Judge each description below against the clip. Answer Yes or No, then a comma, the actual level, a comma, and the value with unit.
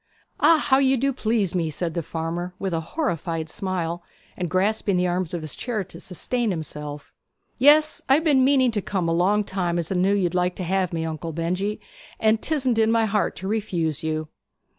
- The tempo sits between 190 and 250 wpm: Yes, fast, 205 wpm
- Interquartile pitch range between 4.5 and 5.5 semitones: Yes, average, 5.0 semitones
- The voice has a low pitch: No, medium, 185 Hz